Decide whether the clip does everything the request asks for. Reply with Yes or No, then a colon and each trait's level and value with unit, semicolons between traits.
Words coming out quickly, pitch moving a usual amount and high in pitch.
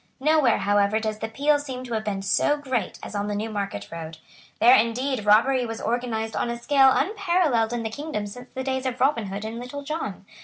Yes: fast, 215 wpm; average, 3.9 semitones; high, 235 Hz